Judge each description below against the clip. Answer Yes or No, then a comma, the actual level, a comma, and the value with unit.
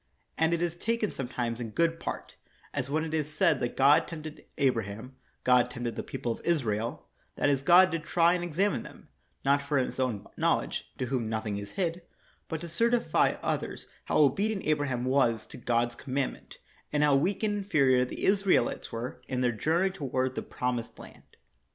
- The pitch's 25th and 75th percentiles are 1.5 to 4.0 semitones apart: No, average, 5.3 semitones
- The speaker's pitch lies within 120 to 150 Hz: Yes, medium, 140 Hz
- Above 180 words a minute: Yes, average, 195 wpm